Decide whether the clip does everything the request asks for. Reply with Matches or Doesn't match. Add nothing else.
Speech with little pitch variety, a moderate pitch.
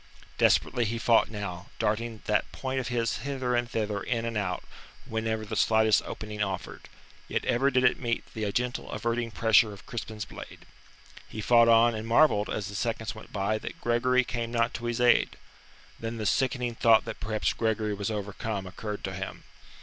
Doesn't match